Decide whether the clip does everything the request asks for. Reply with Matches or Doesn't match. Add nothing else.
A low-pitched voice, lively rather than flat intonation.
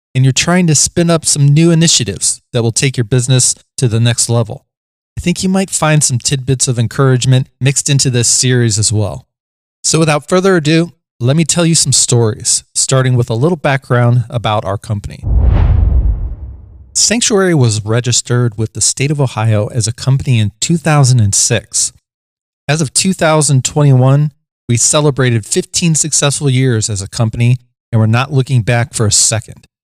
Doesn't match